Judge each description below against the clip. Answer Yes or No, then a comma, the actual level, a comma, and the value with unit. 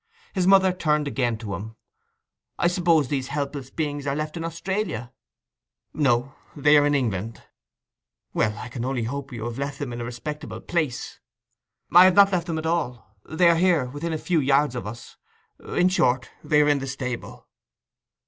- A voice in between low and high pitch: Yes, medium, 145 Hz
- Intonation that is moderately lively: Yes, average, 5.0 semitones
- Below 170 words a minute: No, average, 175 wpm